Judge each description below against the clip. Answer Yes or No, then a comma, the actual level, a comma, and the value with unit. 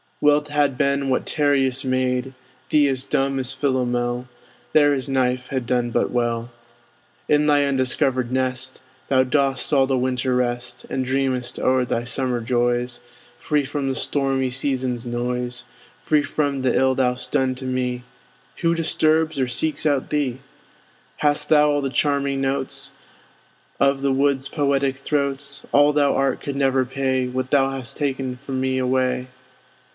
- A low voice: Yes, low, 130 Hz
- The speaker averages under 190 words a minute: Yes, average, 160 wpm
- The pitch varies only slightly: Yes, narrow, 1.8 semitones